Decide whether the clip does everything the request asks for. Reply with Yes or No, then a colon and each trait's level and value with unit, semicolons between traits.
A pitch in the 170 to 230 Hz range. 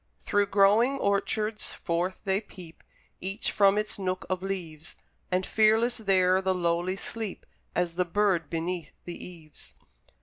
Yes: high, 190 Hz